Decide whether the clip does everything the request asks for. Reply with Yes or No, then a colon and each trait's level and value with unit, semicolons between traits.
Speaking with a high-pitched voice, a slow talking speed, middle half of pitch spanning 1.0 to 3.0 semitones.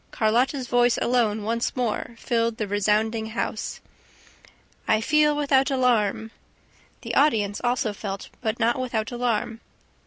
Yes: high, 230 Hz; slow, 130 wpm; narrow, 2.4 semitones